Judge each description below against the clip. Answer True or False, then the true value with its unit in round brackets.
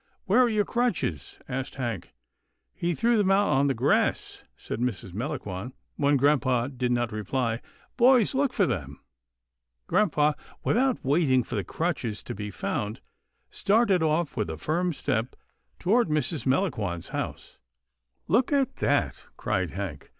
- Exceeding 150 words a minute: True (160 wpm)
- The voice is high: False (140 Hz)